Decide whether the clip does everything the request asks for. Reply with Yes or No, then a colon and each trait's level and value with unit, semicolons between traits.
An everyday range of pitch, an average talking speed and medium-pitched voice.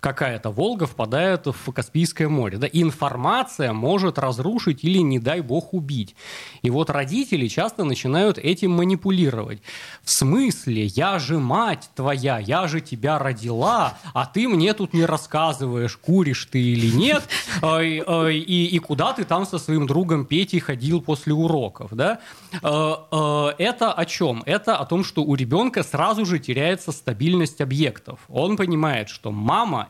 Yes: average, 4.6 semitones; average, 150 wpm; medium, 155 Hz